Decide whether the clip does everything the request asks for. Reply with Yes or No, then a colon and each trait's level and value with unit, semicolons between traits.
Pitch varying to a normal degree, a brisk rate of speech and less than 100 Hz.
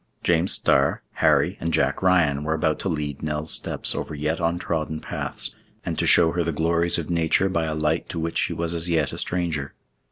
No: narrow, 1.8 semitones; fast, 210 wpm; very low, 80 Hz